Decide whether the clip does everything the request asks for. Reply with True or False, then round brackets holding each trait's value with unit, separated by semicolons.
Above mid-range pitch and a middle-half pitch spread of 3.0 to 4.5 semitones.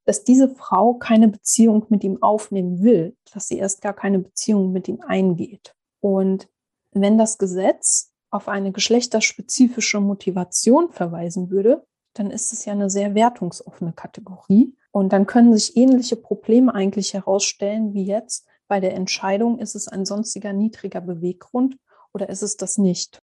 False (205 Hz; 2.6 semitones)